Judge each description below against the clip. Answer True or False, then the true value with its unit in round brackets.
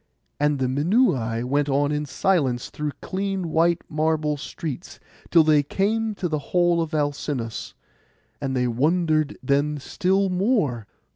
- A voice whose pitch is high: False (150 Hz)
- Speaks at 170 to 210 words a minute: False (140 wpm)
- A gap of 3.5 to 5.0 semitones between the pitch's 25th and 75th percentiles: True (4.1 semitones)